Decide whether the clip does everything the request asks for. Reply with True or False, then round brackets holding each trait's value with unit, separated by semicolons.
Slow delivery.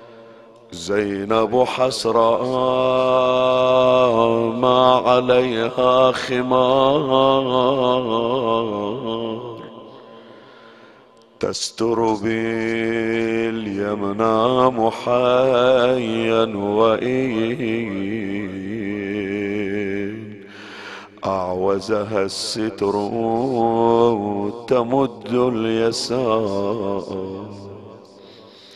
True (25 wpm)